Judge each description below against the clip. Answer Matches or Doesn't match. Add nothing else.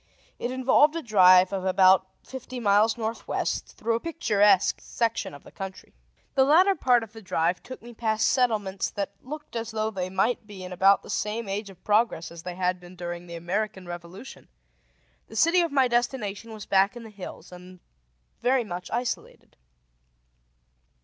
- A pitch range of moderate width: Matches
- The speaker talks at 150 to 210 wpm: Matches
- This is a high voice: Matches